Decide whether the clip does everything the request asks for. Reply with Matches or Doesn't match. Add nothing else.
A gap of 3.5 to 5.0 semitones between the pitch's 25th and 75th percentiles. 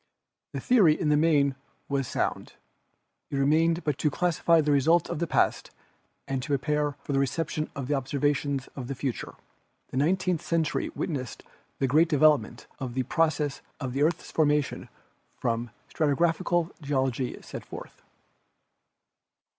Doesn't match